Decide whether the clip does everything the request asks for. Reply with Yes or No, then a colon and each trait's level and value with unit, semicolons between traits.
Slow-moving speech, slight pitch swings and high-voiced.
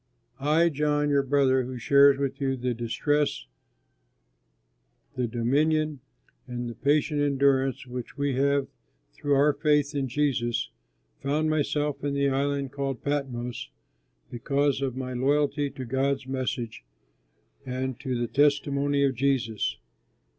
No: slow, 130 wpm; narrow, 2.1 semitones; medium, 140 Hz